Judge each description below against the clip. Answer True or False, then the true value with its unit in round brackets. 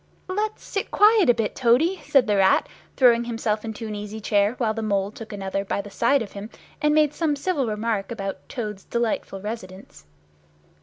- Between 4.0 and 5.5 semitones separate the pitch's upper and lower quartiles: True (4.7 semitones)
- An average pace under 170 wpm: False (190 wpm)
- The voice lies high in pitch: True (225 Hz)